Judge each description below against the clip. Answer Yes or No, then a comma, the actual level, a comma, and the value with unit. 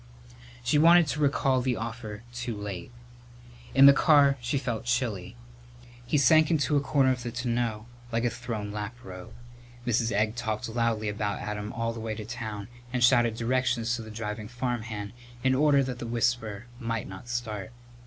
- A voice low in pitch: Yes, low, 120 Hz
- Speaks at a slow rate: No, average, 175 wpm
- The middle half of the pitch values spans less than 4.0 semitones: Yes, average, 2.9 semitones